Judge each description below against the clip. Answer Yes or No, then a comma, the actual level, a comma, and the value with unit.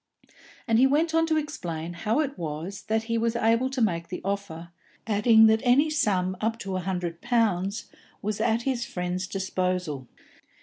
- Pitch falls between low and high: No, high, 210 Hz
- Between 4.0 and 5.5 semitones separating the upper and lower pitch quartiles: Yes, average, 4.6 semitones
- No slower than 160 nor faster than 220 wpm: Yes, average, 175 wpm